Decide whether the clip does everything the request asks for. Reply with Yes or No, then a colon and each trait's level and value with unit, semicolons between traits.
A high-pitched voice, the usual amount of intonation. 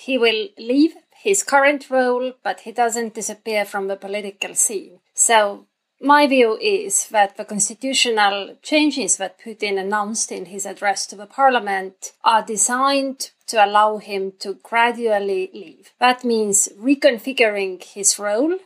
Yes: high, 220 Hz; average, 4.5 semitones